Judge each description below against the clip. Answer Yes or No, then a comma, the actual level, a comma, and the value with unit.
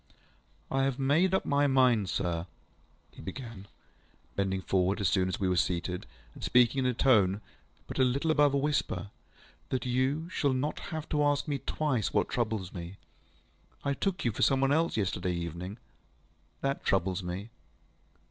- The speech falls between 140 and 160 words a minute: No, average, 170 wpm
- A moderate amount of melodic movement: No, wide, 6.8 semitones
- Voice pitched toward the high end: No, low, 125 Hz